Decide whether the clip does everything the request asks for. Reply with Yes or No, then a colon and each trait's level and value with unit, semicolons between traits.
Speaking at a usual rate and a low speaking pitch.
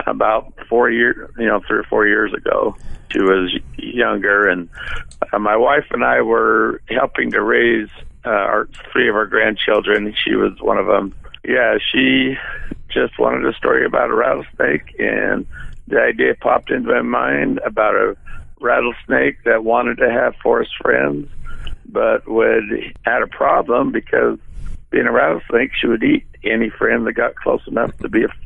Yes: average, 165 wpm; low, 100 Hz